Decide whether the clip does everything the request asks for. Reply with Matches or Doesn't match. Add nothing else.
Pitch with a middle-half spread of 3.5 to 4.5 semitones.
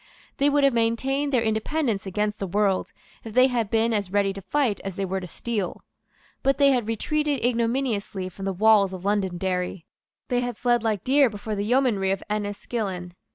Matches